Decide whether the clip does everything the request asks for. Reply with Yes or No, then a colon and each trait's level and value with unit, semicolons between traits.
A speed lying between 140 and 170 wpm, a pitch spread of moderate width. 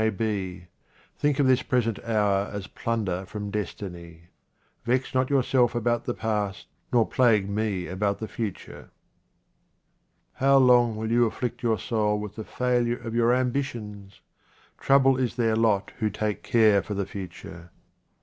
Yes: average, 150 wpm; average, 3.2 semitones